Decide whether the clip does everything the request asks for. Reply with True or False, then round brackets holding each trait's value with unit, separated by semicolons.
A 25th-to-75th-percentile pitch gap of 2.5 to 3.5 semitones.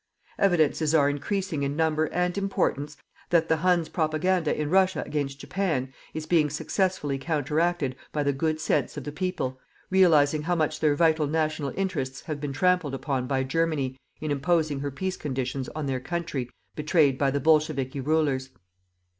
True (3.1 semitones)